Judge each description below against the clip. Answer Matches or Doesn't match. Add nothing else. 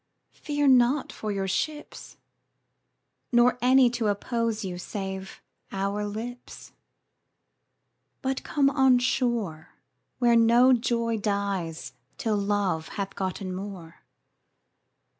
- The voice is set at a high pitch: Matches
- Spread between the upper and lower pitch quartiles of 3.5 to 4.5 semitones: Matches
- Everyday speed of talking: Doesn't match